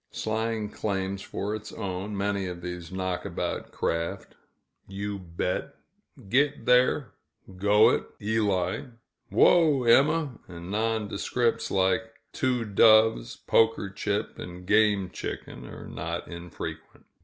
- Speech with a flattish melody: No, average, 3.3 semitones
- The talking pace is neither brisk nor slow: No, slow, 110 wpm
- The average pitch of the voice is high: No, low, 105 Hz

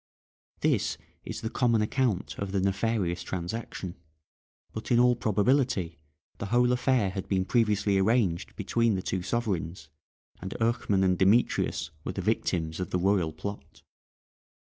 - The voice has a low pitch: Yes, low, 100 Hz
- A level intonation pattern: No, average, 3.9 semitones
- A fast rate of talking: No, average, 145 wpm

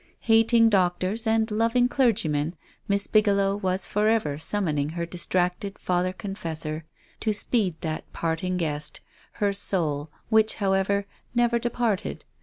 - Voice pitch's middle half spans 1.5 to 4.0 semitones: No, average, 4.5 semitones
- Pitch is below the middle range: No, high, 195 Hz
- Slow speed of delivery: Yes, slow, 130 wpm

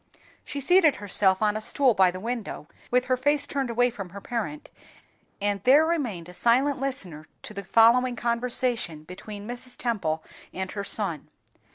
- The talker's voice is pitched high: Yes, high, 230 Hz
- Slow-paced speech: No, average, 170 wpm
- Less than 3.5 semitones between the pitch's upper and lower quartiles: No, average, 4.7 semitones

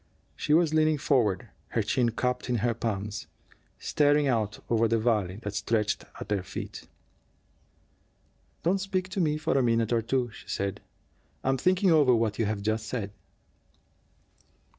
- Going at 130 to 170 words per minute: Yes, average, 160 wpm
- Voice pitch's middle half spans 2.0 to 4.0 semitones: No, wide, 5.4 semitones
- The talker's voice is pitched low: Yes, low, 115 Hz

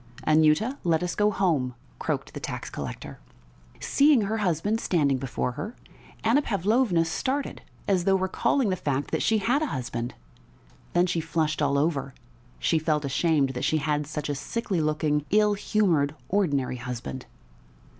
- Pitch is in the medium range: Yes, medium, 165 Hz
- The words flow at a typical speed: Yes, average, 155 wpm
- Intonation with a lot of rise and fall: Yes, wide, 6.1 semitones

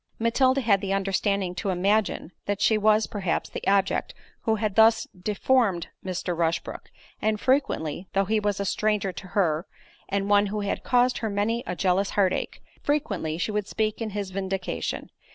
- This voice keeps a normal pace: Yes, average, 175 wpm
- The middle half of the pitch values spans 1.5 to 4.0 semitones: Yes, narrow, 2.4 semitones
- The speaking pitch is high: Yes, high, 200 Hz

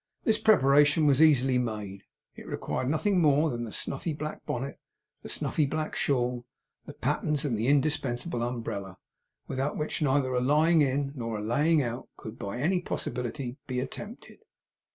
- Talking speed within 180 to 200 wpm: No, average, 165 wpm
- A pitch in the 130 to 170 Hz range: Yes, low, 135 Hz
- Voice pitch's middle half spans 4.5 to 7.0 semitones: No, average, 3.9 semitones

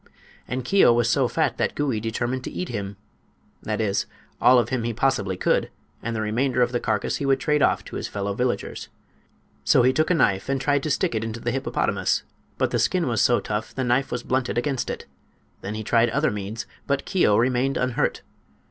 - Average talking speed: No, fast, 210 wpm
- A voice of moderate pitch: No, low, 120 Hz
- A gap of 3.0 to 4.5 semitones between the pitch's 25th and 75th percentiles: Yes, average, 3.5 semitones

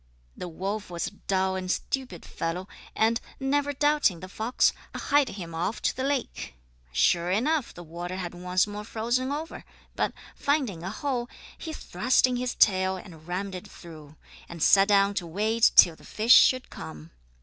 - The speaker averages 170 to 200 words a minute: Yes, average, 175 wpm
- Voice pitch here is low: No, high, 195 Hz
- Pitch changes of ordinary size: No, wide, 6.0 semitones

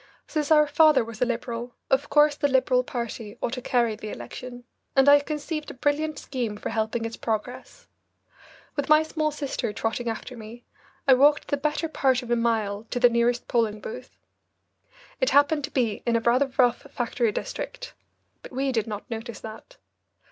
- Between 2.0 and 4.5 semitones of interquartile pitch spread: Yes, average, 3.9 semitones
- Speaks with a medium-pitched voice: No, very high, 250 Hz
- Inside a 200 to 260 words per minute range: No, average, 185 wpm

